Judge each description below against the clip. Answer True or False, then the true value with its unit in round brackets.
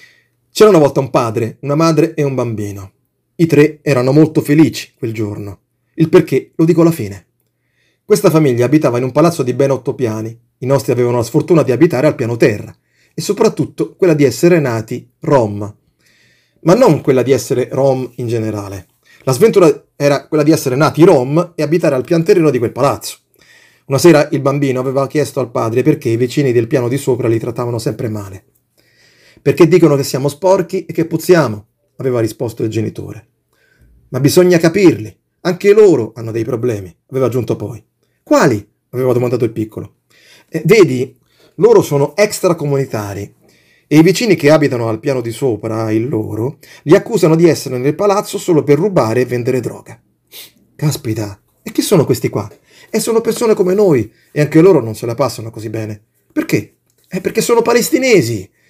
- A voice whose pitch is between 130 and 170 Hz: True (140 Hz)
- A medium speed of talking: False (180 wpm)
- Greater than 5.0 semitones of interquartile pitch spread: True (5.5 semitones)